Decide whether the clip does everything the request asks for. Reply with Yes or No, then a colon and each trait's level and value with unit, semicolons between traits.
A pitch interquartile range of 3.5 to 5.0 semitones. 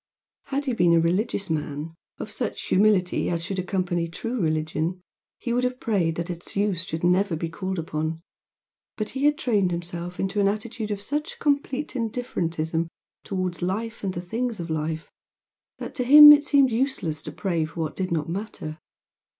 No: wide, 5.4 semitones